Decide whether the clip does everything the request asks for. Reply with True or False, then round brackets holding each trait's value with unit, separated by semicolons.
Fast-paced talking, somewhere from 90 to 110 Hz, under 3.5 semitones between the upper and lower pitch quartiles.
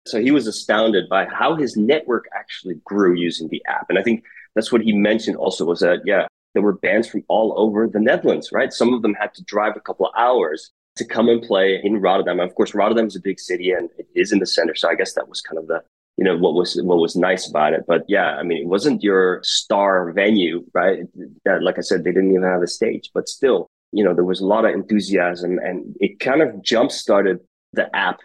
True (250 wpm; 100 Hz; 2.9 semitones)